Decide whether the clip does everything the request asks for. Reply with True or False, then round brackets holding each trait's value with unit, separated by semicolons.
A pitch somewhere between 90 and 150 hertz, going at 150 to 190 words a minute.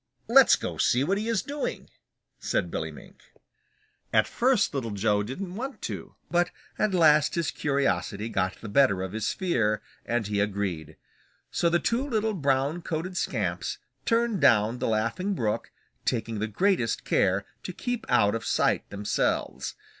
True (140 Hz; 160 wpm)